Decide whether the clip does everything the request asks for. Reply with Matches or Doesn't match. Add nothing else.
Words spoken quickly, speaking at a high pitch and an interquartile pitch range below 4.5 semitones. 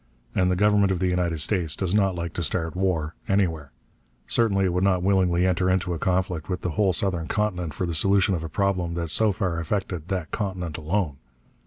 Doesn't match